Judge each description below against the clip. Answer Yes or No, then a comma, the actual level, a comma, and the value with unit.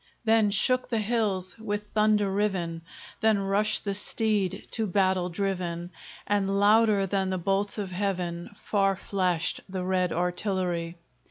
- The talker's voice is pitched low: No, high, 195 Hz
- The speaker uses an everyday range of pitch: No, narrow, 2.3 semitones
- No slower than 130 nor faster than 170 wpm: Yes, average, 140 wpm